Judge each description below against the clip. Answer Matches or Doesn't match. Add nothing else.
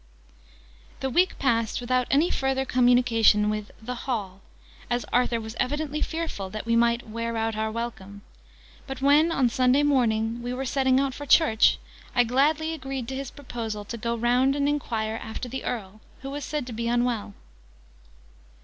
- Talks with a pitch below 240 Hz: Doesn't match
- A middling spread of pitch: Matches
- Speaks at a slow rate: Doesn't match